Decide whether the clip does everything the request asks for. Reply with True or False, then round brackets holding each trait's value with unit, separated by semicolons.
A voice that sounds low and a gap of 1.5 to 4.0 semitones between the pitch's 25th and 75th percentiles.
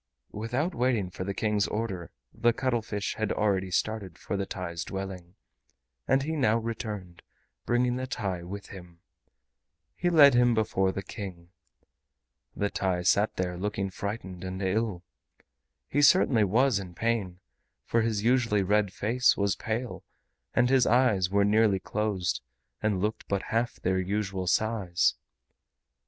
True (105 Hz; 3.6 semitones)